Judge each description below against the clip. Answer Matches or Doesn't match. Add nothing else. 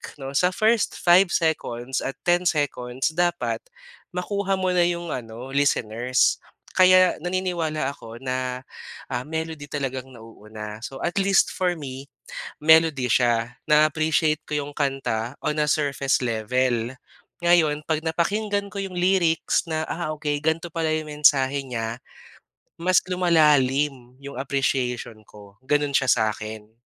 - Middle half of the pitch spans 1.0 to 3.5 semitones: Doesn't match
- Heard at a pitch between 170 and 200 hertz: Doesn't match